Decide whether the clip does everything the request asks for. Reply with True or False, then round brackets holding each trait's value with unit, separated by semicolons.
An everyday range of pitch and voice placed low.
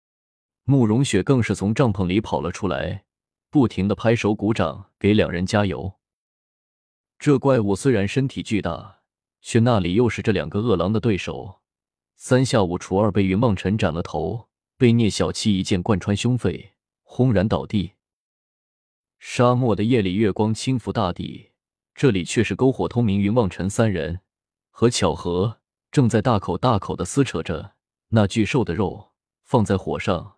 True (3.8 semitones; 105 Hz)